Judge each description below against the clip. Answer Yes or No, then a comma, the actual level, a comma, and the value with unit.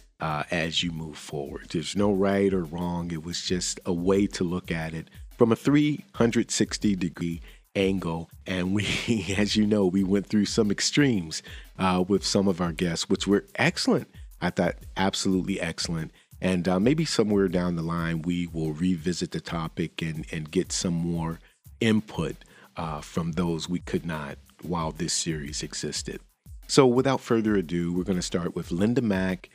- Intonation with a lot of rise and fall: No, average, 3.0 semitones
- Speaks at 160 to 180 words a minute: Yes, average, 175 wpm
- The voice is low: Yes, very low, 90 Hz